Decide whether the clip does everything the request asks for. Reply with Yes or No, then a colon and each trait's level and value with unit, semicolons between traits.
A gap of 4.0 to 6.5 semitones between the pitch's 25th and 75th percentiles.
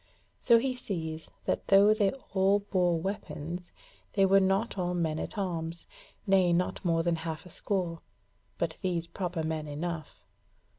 No: average, 3.0 semitones